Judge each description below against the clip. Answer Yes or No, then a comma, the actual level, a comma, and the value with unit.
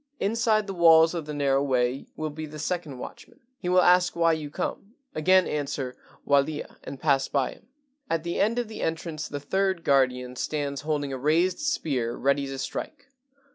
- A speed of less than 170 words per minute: No, average, 185 wpm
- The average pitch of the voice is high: No, medium, 155 Hz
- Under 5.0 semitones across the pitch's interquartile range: Yes, average, 4.3 semitones